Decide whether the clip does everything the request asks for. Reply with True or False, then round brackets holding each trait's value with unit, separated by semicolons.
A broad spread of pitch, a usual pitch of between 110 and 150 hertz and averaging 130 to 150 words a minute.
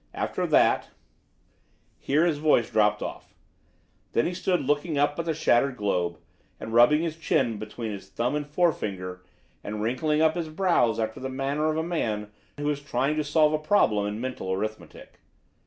False (6.2 semitones; 140 Hz; 180 wpm)